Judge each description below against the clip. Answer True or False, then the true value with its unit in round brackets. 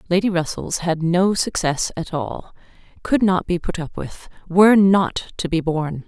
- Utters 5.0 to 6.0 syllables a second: False (4.5 syllables/s)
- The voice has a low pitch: False (175 Hz)